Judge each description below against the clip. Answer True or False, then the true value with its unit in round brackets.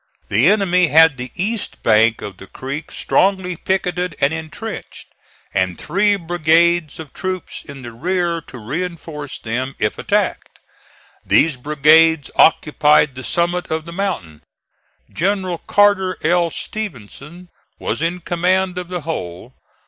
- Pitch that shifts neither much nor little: True (4.6 semitones)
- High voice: False (165 Hz)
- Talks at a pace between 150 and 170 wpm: False (135 wpm)